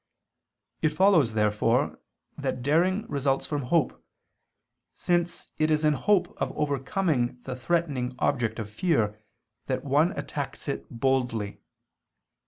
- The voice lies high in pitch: No, medium, 140 Hz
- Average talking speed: No, slow, 125 wpm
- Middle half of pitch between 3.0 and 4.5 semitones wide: No, wide, 5.5 semitones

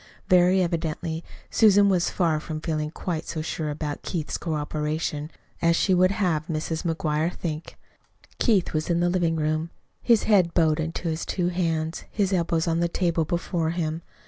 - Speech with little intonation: Yes, narrow, 2.1 semitones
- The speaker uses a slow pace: No, average, 170 wpm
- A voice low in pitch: No, medium, 165 Hz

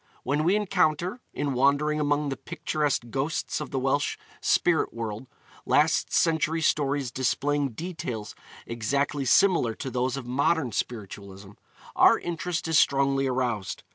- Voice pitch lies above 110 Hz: Yes, medium, 140 Hz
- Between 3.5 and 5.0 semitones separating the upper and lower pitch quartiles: Yes, average, 3.8 semitones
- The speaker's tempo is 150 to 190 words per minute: No, slow, 135 wpm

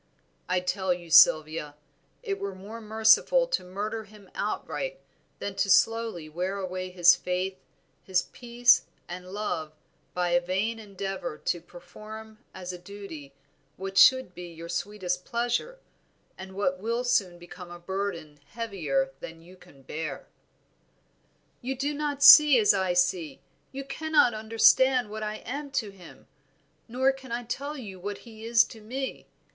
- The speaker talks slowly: No, average, 150 wpm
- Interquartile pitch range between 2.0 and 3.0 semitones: No, average, 4.8 semitones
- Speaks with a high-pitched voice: Yes, high, 200 Hz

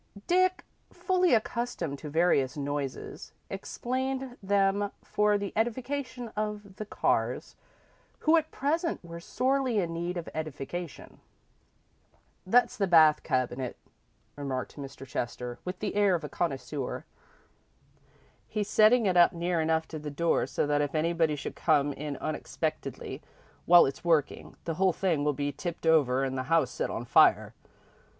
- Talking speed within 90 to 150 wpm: Yes, average, 145 wpm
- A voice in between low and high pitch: Yes, medium, 170 Hz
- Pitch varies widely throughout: Yes, wide, 6.4 semitones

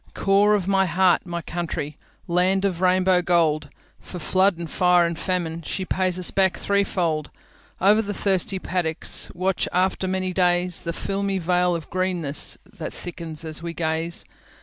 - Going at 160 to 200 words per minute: No, slow, 135 wpm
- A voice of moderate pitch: Yes, medium, 180 Hz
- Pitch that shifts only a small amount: Yes, narrow, 2.0 semitones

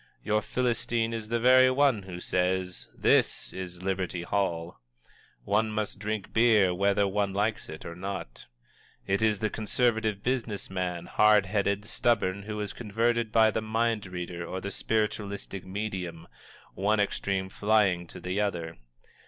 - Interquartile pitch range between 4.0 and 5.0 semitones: No, average, 2.8 semitones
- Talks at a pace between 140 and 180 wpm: Yes, average, 155 wpm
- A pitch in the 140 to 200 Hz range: No, low, 100 Hz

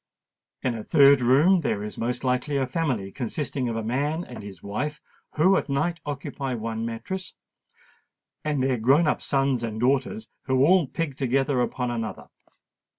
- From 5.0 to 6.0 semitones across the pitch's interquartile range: No, average, 3.8 semitones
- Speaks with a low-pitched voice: Yes, low, 130 Hz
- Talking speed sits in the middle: Yes, average, 165 wpm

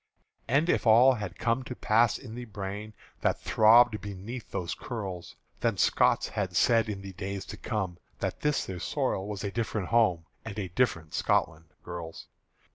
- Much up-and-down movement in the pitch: No, average, 3.7 semitones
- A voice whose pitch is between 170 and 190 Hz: No, low, 105 Hz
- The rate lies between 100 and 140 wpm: No, average, 175 wpm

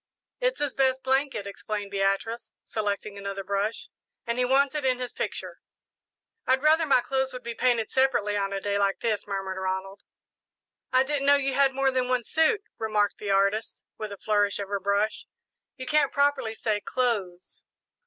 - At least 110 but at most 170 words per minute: No, average, 180 wpm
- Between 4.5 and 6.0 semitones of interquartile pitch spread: Yes, average, 4.9 semitones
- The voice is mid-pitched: No, high, 225 Hz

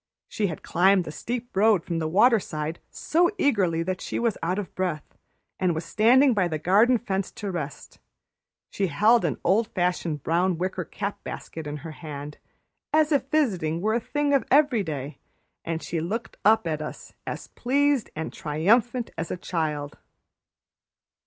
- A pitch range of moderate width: No, wide, 6.2 semitones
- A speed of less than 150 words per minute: No, average, 165 wpm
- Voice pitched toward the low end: No, medium, 185 Hz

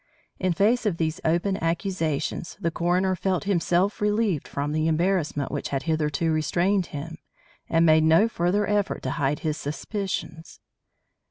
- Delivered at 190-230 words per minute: No, average, 150 wpm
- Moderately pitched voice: Yes, medium, 170 Hz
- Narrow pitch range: No, average, 3.5 semitones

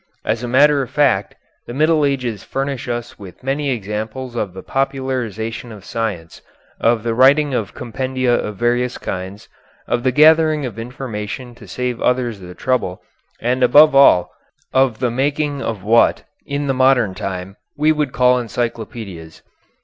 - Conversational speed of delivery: Yes, average, 155 wpm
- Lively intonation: No, average, 3.5 semitones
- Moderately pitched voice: No, low, 125 Hz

